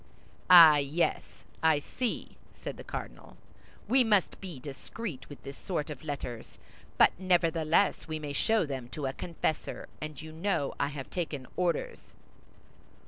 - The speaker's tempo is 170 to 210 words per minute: No, average, 145 wpm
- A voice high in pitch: No, medium, 155 Hz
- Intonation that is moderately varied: Yes, average, 4.1 semitones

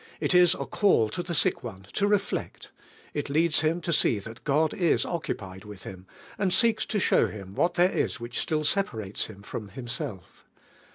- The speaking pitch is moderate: Yes, medium, 150 Hz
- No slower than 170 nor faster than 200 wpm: Yes, average, 190 wpm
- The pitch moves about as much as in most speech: No, wide, 9.0 semitones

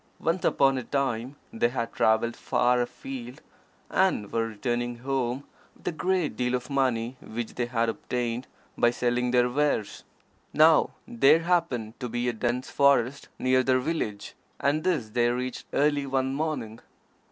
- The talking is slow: No, average, 155 wpm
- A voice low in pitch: Yes, low, 125 Hz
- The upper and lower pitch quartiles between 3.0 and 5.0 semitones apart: No, narrow, 2.6 semitones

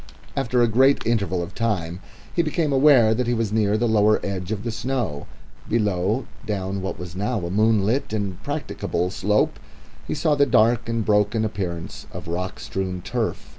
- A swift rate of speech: No, average, 175 wpm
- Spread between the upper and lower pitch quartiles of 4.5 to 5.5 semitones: No, average, 3.8 semitones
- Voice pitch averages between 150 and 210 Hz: No, low, 110 Hz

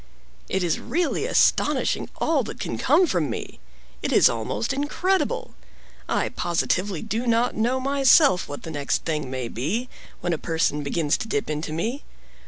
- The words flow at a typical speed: Yes, average, 165 wpm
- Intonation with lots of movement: Yes, wide, 8.6 semitones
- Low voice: No, medium, 180 Hz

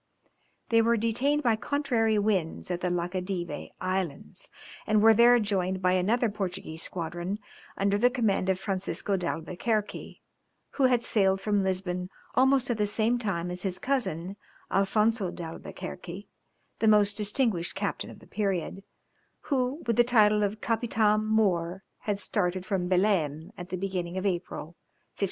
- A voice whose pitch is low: No, high, 200 Hz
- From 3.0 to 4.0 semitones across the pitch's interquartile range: Yes, average, 3.5 semitones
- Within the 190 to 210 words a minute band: No, average, 150 wpm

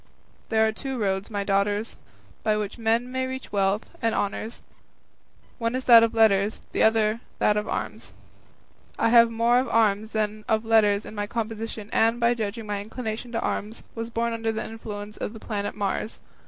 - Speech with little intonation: Yes, narrow, 1.7 semitones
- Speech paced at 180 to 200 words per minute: Yes, average, 185 wpm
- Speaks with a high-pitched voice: Yes, high, 220 Hz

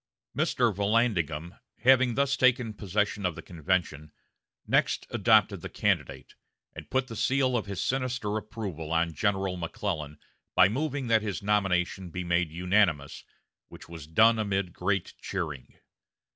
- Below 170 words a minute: Yes, average, 140 wpm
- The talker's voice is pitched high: No, low, 100 Hz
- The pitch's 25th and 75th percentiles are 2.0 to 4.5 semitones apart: No, average, 4.9 semitones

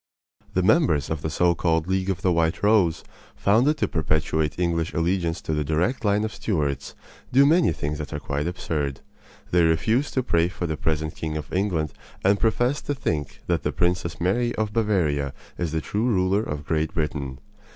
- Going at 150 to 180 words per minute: No, average, 190 wpm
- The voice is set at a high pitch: No, very low, 85 Hz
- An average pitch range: Yes, average, 4.9 semitones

